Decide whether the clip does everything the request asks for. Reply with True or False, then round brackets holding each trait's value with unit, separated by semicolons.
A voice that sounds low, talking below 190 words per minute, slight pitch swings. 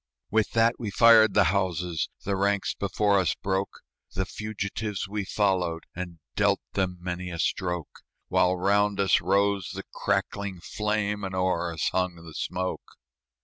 True (95 Hz; 150 wpm; 2.2 semitones)